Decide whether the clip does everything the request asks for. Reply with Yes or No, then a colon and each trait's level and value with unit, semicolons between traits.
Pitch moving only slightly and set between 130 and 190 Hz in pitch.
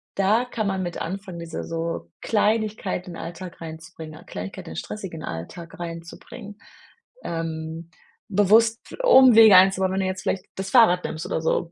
No: average, 3.9 semitones; medium, 185 Hz